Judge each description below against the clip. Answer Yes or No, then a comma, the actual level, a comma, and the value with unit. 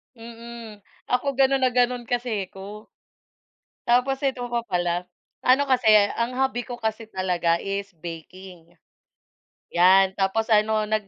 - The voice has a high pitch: Yes, high, 220 Hz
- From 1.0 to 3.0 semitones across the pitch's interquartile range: No, average, 4.3 semitones